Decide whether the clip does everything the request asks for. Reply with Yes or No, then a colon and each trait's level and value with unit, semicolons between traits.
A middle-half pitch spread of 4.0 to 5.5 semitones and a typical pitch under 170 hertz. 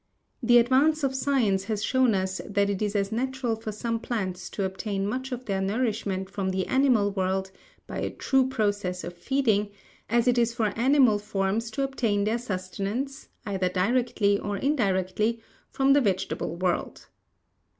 No: average, 4.4 semitones; high, 215 Hz